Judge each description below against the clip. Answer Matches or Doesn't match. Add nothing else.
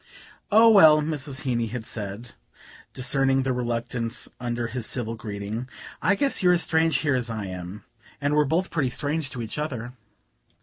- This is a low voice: Matches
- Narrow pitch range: Doesn't match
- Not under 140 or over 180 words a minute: Matches